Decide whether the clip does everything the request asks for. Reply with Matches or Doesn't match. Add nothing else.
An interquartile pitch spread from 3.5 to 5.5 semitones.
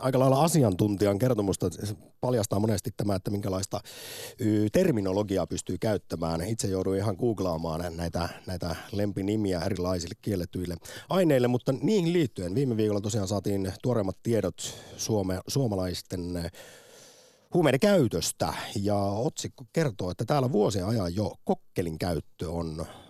Matches